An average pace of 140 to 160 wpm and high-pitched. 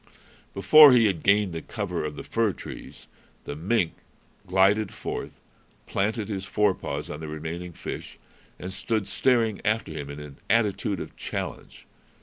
No: average, 150 wpm; low, 100 Hz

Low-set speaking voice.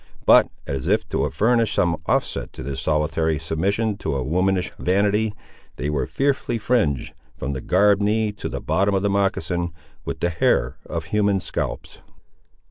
Yes: very low, 95 Hz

